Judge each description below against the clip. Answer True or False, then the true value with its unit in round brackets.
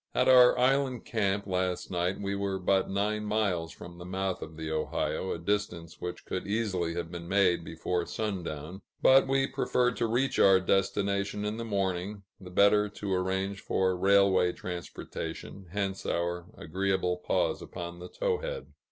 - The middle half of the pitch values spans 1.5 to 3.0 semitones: True (2.7 semitones)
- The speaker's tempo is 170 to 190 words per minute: False (160 wpm)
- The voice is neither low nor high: False (95 Hz)